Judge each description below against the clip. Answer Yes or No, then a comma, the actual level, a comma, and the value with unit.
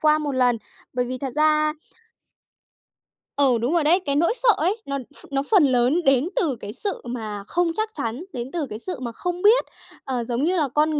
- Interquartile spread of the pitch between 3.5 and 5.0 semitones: No, wide, 5.4 semitones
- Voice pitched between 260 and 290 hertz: Yes, very high, 285 Hz